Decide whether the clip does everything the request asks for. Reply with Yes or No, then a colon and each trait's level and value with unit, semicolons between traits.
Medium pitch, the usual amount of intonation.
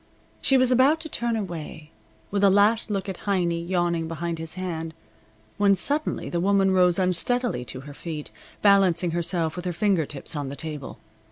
Yes: medium, 180 Hz; average, 3.7 semitones